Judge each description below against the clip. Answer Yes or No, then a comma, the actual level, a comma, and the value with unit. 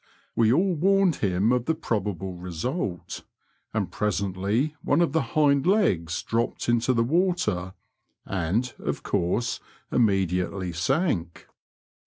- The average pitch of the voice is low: Yes, low, 115 Hz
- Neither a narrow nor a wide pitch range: No, wide, 8.0 semitones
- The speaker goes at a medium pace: No, slow, 120 wpm